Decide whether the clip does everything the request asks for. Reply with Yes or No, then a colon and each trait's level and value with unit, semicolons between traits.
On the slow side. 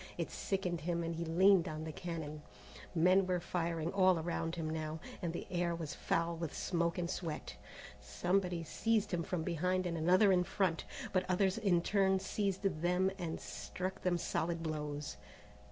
No: average, 170 wpm